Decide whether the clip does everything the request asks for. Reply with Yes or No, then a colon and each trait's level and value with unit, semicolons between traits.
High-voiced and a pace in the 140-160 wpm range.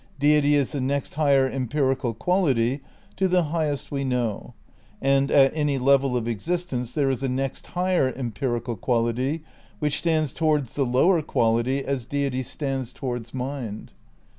No: low, 135 Hz; average, 155 wpm